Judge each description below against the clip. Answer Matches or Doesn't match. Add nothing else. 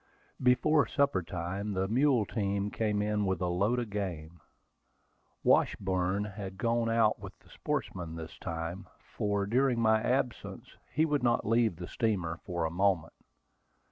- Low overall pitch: Matches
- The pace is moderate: Matches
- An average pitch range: Matches